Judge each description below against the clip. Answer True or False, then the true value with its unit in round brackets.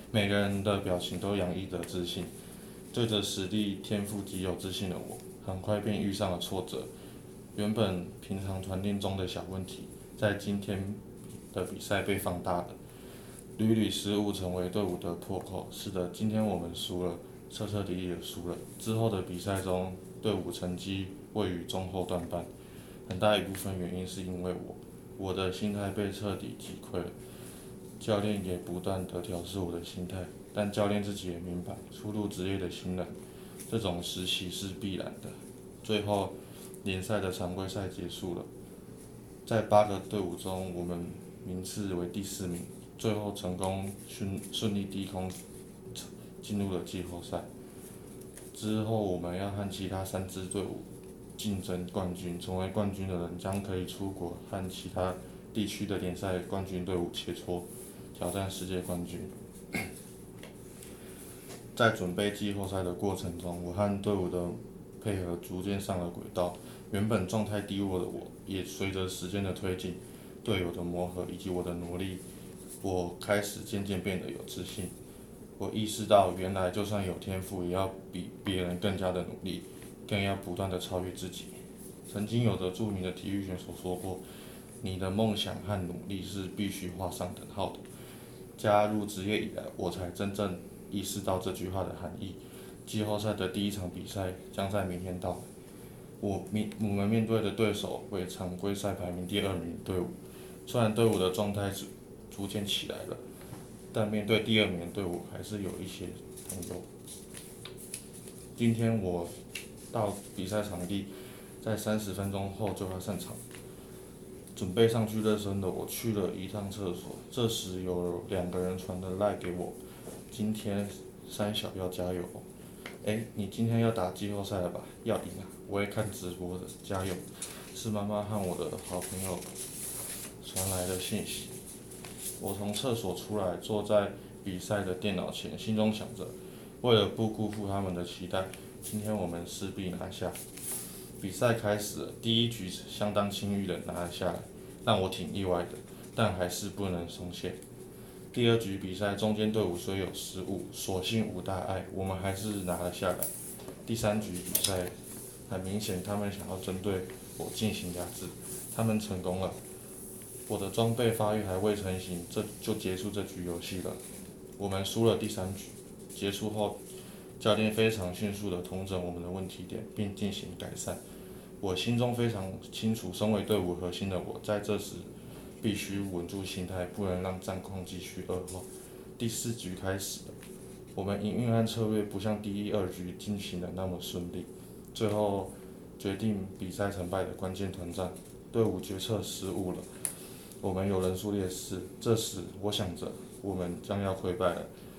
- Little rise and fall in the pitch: True (2.3 semitones)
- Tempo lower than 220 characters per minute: False (245 characters per minute)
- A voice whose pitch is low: True (95 Hz)